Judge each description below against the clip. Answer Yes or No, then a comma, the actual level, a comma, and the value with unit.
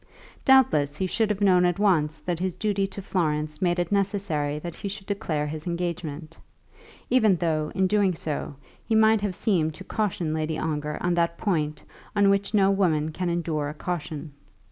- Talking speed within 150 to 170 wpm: No, average, 185 wpm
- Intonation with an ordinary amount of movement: Yes, average, 4.3 semitones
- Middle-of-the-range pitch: Yes, medium, 175 Hz